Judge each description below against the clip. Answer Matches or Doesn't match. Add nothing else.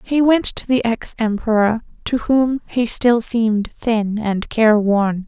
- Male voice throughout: Doesn't match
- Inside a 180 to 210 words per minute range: Doesn't match